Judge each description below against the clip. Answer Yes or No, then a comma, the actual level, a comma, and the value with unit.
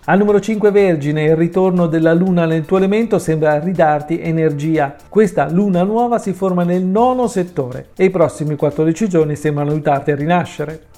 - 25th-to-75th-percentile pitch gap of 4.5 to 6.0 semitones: No, average, 3.8 semitones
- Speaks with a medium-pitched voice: Yes, medium, 170 Hz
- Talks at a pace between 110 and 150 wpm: No, fast, 170 wpm